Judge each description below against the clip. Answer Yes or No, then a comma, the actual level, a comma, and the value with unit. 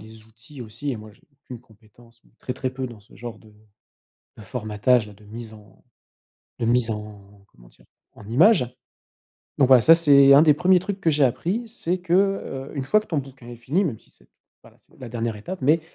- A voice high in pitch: No, low, 125 Hz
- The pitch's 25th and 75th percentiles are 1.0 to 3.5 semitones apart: No, average, 5.3 semitones